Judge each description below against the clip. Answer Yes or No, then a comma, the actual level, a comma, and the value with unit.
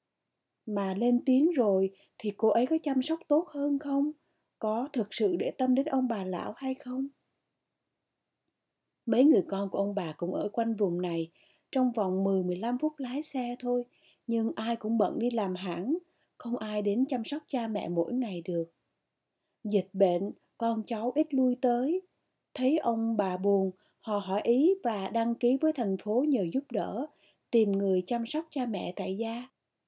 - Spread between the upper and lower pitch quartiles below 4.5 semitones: No, average, 4.8 semitones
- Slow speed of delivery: No, average, 180 wpm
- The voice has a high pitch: Yes, high, 230 Hz